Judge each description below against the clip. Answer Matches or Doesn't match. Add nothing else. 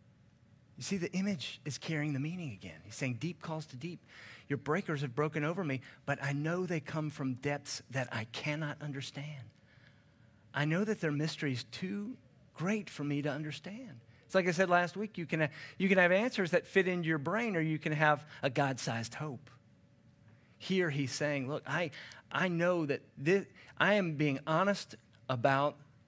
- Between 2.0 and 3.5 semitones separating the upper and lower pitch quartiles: Doesn't match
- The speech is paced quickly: Doesn't match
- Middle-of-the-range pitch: Matches